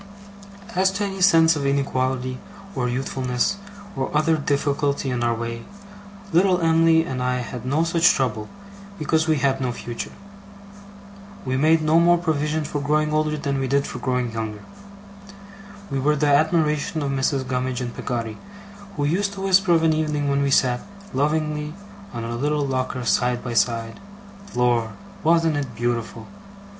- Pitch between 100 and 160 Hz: Yes, medium, 140 Hz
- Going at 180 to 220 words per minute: No, average, 160 wpm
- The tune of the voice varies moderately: Yes, average, 3.9 semitones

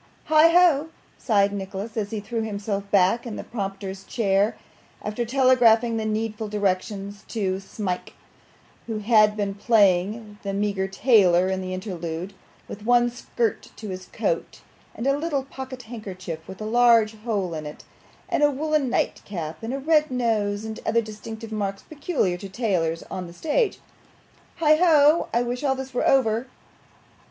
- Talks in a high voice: Yes, high, 215 Hz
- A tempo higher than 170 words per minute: No, average, 155 wpm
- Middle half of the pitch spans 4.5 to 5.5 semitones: No, average, 3.8 semitones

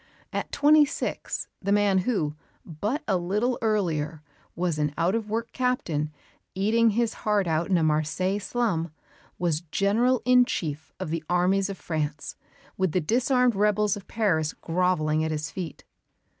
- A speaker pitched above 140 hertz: Yes, high, 190 Hz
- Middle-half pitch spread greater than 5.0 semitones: Yes, wide, 5.5 semitones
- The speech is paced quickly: No, average, 155 wpm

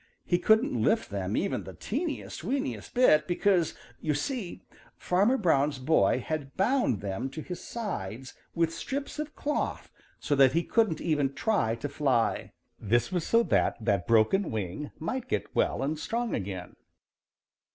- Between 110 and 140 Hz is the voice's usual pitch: No, medium, 160 Hz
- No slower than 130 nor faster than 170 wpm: Yes, average, 155 wpm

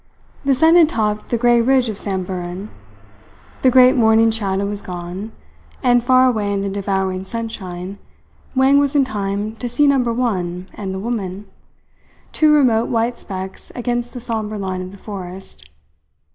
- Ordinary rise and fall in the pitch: Yes, average, 4.2 semitones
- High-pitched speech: Yes, high, 215 Hz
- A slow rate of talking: No, average, 160 wpm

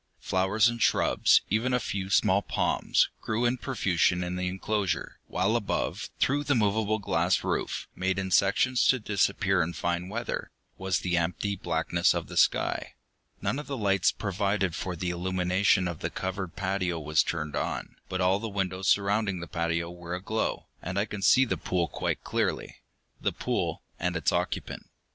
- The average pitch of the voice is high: No, very low, 95 Hz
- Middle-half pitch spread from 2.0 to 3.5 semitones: Yes, average, 2.9 semitones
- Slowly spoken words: No, average, 175 wpm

